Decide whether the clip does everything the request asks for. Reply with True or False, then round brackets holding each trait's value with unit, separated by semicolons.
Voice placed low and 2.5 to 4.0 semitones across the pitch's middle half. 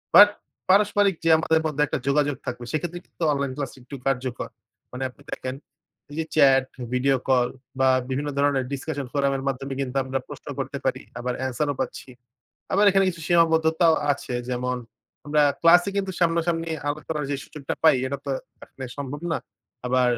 False (145 Hz; 3.6 semitones)